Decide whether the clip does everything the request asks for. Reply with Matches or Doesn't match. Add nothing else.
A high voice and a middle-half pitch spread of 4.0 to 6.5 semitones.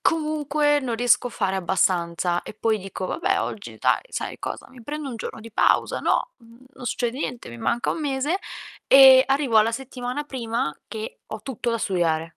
Matches